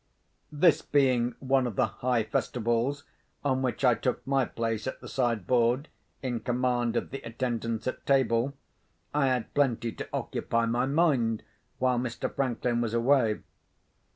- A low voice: Yes, low, 125 Hz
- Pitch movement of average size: No, narrow, 2.3 semitones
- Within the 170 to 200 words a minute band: No, average, 155 wpm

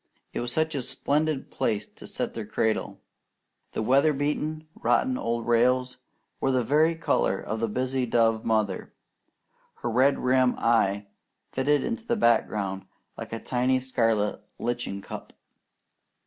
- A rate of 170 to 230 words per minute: No, average, 140 wpm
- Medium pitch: No, low, 125 Hz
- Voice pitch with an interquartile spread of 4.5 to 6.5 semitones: No, average, 3.7 semitones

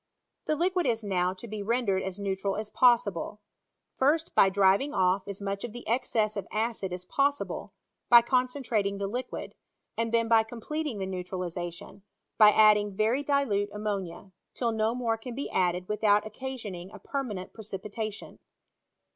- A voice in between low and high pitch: No, high, 215 Hz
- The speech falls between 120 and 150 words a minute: No, average, 160 wpm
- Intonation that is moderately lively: Yes, average, 3.6 semitones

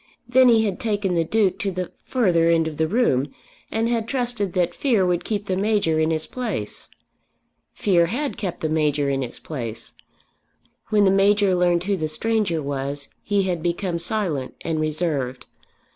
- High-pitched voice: No, medium, 180 Hz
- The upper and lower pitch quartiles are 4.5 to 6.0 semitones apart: Yes, average, 4.9 semitones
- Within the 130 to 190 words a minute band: Yes, average, 175 wpm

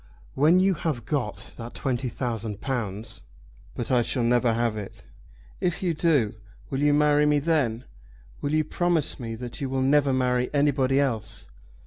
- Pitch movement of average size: Yes, average, 4.0 semitones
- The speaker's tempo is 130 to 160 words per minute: No, average, 170 wpm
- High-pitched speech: No, low, 130 Hz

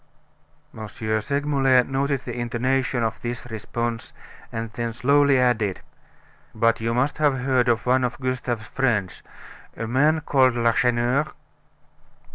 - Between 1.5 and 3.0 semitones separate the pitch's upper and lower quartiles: Yes, narrow, 2.6 semitones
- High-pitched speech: No, low, 125 Hz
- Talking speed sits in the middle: No, slow, 125 wpm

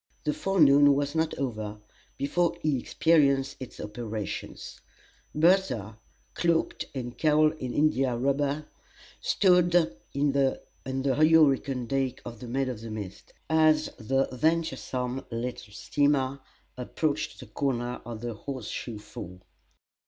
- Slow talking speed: Yes, slow, 125 wpm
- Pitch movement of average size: Yes, average, 4.1 semitones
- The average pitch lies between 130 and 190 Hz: Yes, low, 135 Hz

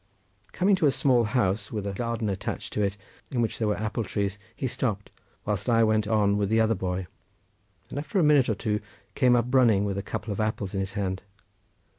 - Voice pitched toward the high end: No, low, 110 Hz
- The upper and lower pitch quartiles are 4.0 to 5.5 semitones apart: No, average, 2.9 semitones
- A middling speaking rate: No, fast, 220 wpm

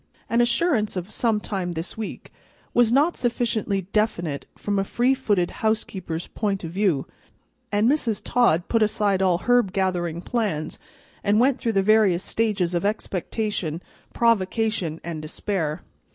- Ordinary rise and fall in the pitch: Yes, average, 4.3 semitones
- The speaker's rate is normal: Yes, average, 145 wpm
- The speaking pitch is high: Yes, high, 205 Hz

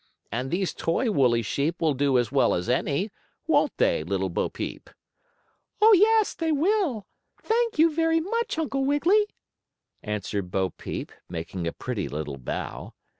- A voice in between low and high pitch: Yes, medium, 165 Hz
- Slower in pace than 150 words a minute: No, average, 155 wpm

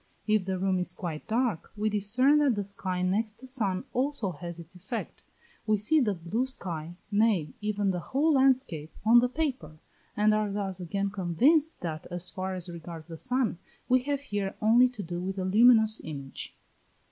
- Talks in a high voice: Yes, high, 205 Hz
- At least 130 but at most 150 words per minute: No, average, 185 wpm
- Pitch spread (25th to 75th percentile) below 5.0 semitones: No, wide, 5.4 semitones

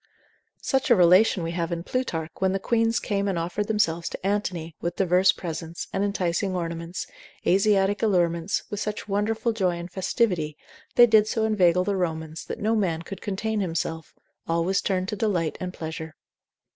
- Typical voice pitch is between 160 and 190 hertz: Yes, medium, 185 Hz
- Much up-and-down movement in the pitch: No, average, 3.6 semitones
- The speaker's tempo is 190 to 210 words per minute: No, average, 175 wpm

